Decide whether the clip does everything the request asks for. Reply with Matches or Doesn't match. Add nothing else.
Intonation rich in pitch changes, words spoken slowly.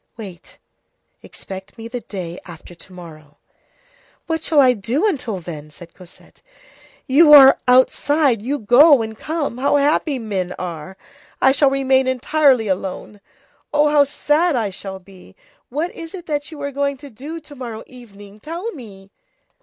Doesn't match